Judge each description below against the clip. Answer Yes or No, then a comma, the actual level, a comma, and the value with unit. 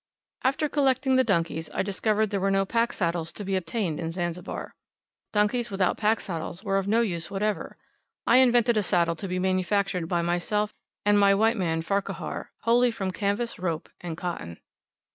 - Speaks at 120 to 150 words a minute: No, average, 180 wpm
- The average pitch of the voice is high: Yes, high, 195 Hz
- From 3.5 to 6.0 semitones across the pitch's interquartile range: Yes, average, 4.2 semitones